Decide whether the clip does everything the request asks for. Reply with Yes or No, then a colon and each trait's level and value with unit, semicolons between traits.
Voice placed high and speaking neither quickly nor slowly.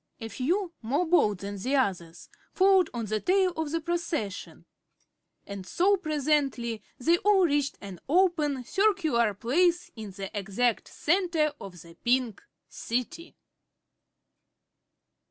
No: very high, 280 Hz; slow, 130 wpm